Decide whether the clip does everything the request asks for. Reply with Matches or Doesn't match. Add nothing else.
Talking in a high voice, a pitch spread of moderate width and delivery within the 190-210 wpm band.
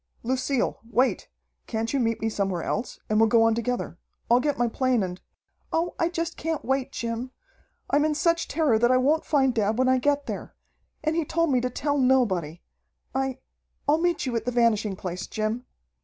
Matches